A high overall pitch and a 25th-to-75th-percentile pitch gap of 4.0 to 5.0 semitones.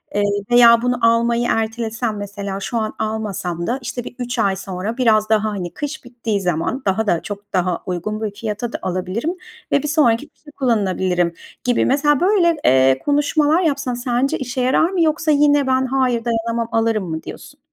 Yes: high, 230 Hz; average, 4.4 semitones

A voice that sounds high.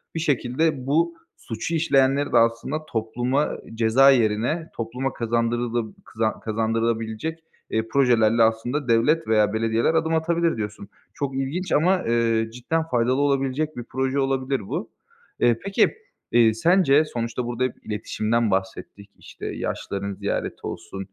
No: low, 120 Hz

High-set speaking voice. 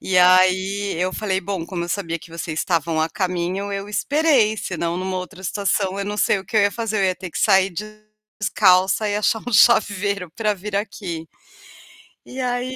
Yes: high, 195 Hz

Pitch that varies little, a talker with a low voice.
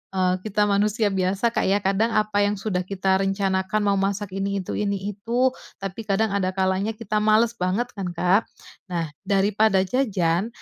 No: narrow, 2.0 semitones; high, 200 Hz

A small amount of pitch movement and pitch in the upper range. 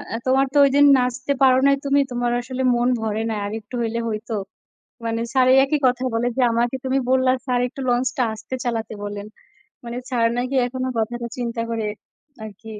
Yes: narrow, 2.2 semitones; high, 245 Hz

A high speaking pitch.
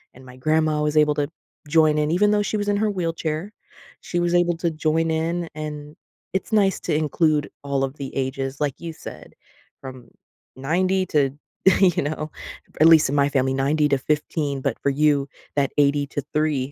No: medium, 150 Hz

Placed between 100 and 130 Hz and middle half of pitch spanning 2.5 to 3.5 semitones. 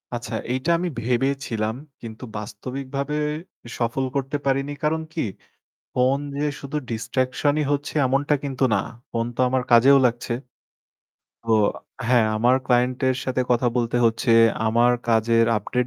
Yes: low, 125 Hz; average, 2.8 semitones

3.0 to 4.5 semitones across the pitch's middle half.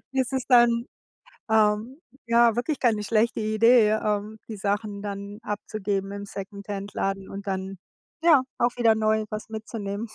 No: narrow, 2.5 semitones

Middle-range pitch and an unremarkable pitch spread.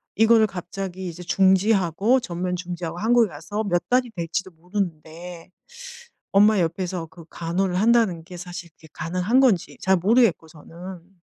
Yes: medium, 180 Hz; average, 3.2 semitones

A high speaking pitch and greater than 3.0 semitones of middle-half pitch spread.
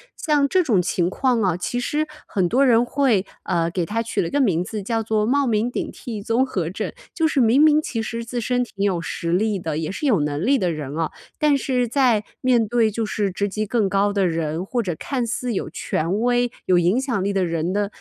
Yes: high, 215 Hz; average, 5.2 semitones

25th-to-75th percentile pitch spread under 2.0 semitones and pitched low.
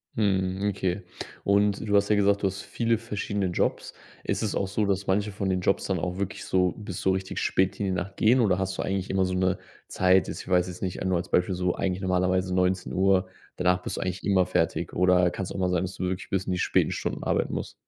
Yes: narrow, 1.4 semitones; very low, 95 Hz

